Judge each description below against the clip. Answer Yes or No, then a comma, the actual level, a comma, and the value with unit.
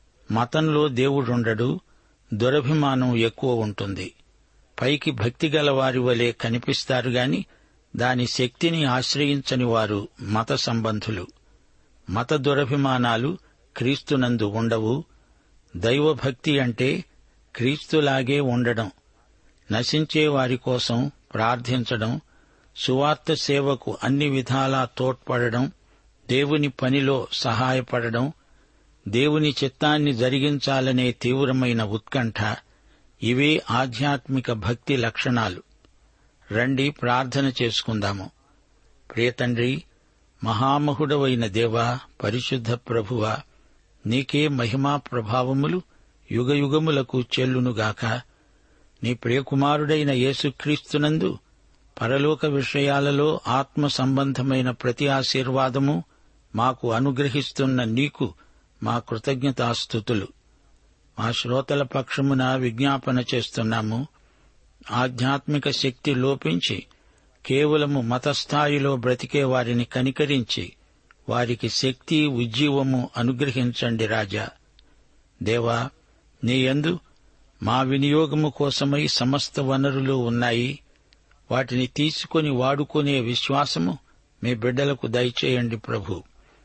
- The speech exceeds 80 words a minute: No, average, 75 wpm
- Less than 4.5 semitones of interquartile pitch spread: Yes, average, 2.9 semitones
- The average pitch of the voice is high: No, low, 130 Hz